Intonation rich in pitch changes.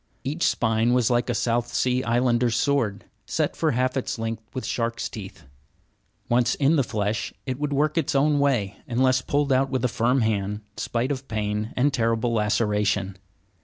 No: average, 3.1 semitones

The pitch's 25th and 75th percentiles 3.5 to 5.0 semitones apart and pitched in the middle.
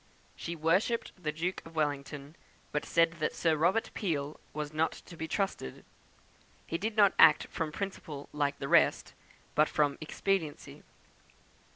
No: average, 3.1 semitones; medium, 160 Hz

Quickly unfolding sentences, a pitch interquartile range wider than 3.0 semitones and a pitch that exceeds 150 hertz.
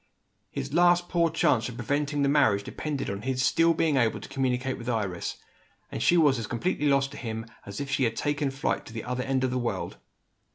No: fast, 220 wpm; average, 3.8 semitones; low, 135 Hz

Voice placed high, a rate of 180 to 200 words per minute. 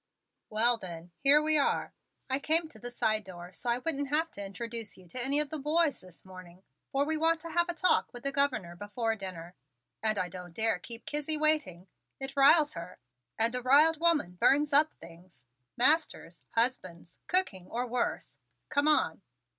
Yes: high, 245 Hz; average, 185 wpm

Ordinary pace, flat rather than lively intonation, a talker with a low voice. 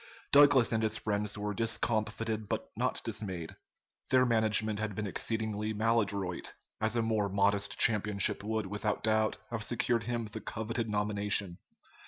Yes: average, 145 wpm; narrow, 1.4 semitones; low, 110 Hz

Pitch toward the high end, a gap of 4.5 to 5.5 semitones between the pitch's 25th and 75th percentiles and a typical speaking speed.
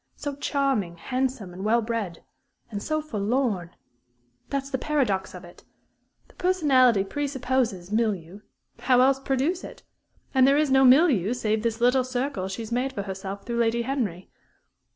Yes: high, 245 Hz; average, 5.1 semitones; average, 160 wpm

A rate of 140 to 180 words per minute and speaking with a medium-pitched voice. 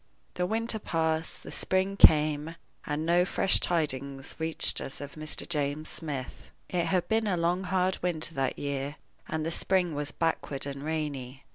Yes: average, 165 wpm; medium, 160 Hz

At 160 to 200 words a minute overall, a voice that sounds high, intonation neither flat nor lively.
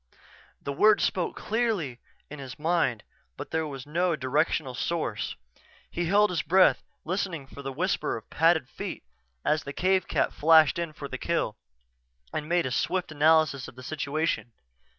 No: average, 170 wpm; medium, 155 Hz; average, 3.8 semitones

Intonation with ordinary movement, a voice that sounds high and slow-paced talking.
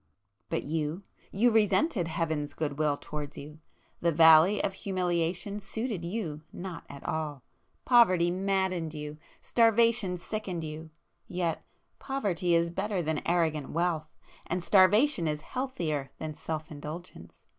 No: average, 3.9 semitones; medium, 170 Hz; slow, 115 wpm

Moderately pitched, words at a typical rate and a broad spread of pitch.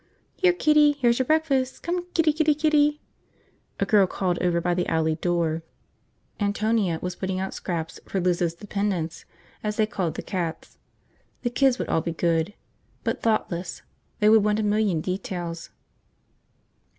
No: high, 200 Hz; average, 155 wpm; wide, 6.9 semitones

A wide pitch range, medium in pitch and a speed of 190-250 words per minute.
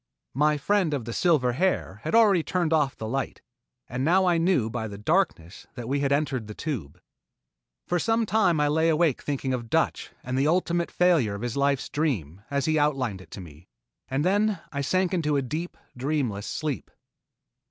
Yes: wide, 5.7 semitones; medium, 145 Hz; average, 195 wpm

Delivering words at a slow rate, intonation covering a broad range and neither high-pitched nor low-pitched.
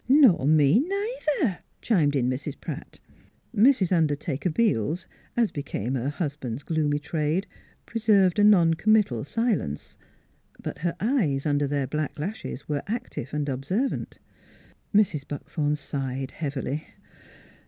Yes: slow, 130 wpm; wide, 6.7 semitones; medium, 155 Hz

